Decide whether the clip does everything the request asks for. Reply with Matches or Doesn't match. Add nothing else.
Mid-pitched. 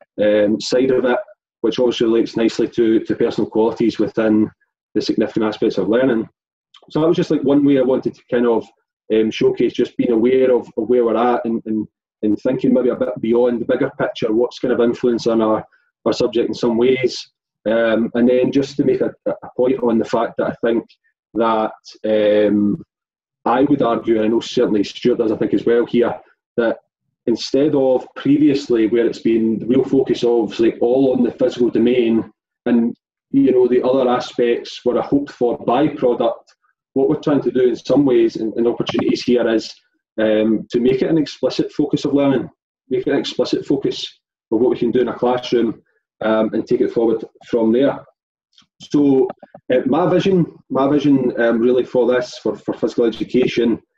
Doesn't match